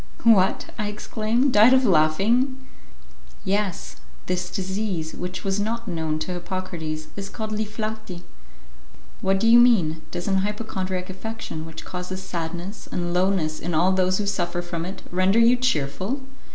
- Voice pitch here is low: No, high, 190 Hz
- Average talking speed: Yes, average, 150 wpm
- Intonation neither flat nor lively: Yes, average, 3.7 semitones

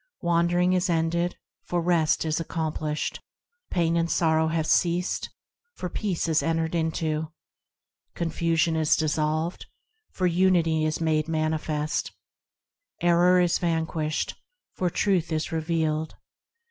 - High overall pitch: No, medium, 165 Hz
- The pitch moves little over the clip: Yes, narrow, 1.5 semitones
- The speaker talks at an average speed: No, slow, 115 wpm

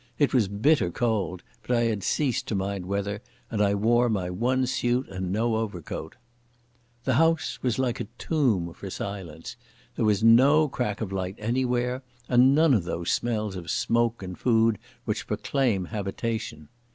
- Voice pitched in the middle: No, low, 110 Hz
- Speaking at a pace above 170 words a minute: No, average, 165 wpm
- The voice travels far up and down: No, average, 4.1 semitones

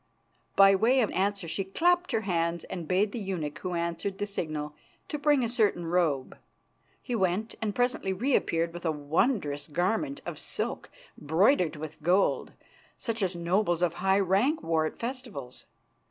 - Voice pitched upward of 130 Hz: Yes, high, 190 Hz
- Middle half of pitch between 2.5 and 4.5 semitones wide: No, average, 4.9 semitones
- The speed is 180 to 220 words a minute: No, average, 165 wpm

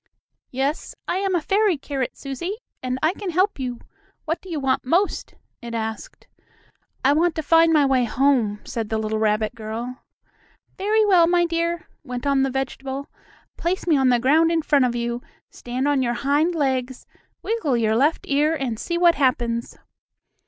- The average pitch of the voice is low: No, very high, 275 Hz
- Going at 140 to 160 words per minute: No, average, 180 wpm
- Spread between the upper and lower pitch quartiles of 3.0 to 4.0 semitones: No, average, 5.2 semitones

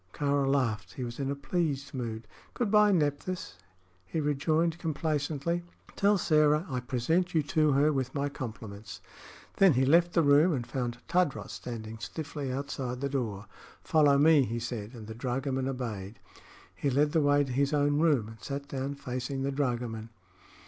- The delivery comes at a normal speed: Yes, average, 170 wpm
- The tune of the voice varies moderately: Yes, average, 3.6 semitones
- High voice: No, medium, 140 Hz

